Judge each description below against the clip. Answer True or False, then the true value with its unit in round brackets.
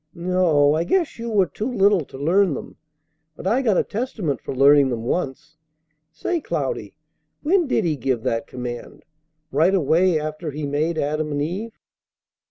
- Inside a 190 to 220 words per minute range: False (170 wpm)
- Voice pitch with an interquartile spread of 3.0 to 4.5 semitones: False (5.6 semitones)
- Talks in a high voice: False (160 Hz)